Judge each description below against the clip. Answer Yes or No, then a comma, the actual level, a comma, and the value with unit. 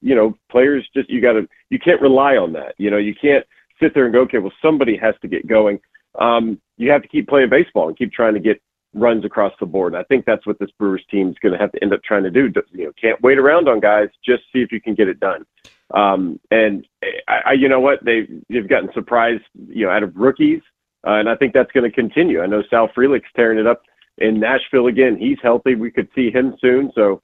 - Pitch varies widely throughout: No, average, 4.1 semitones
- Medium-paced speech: No, fast, 255 wpm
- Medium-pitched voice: No, low, 120 Hz